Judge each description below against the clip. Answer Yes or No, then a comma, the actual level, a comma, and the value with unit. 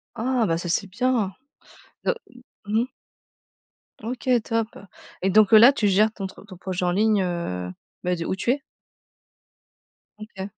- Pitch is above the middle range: Yes, high, 210 Hz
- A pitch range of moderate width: Yes, average, 3.6 semitones